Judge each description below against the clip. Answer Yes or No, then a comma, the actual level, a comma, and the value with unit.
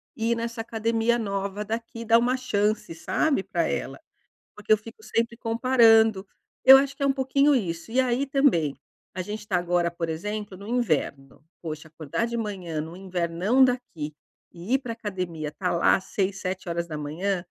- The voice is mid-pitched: No, high, 210 Hz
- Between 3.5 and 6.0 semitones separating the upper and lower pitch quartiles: Yes, average, 5.1 semitones